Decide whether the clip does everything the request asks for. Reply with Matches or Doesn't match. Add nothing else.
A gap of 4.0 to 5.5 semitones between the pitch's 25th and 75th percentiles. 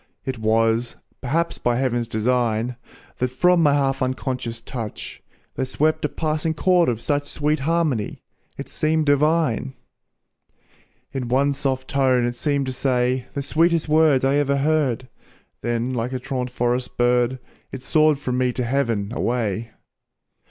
Doesn't match